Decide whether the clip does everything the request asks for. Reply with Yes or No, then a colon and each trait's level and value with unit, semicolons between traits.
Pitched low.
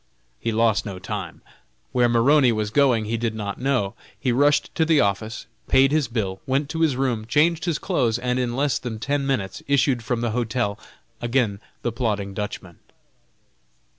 Yes: low, 120 Hz